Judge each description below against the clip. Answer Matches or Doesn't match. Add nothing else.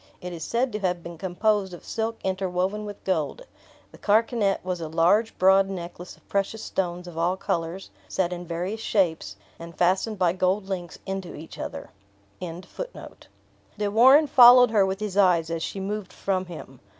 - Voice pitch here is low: Doesn't match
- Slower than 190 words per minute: Matches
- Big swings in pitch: Doesn't match